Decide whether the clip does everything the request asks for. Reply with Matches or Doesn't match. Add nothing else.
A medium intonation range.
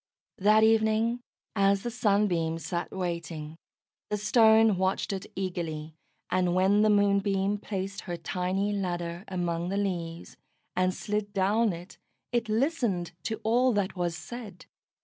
Matches